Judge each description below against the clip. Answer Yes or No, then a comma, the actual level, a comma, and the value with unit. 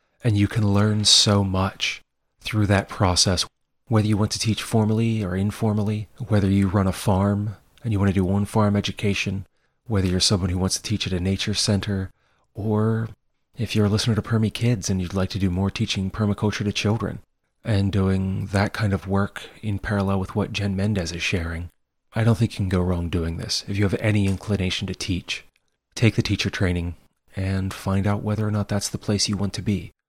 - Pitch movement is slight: Yes, narrow, 1.9 semitones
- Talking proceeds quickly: Yes, fast, 210 wpm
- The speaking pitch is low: Yes, low, 100 Hz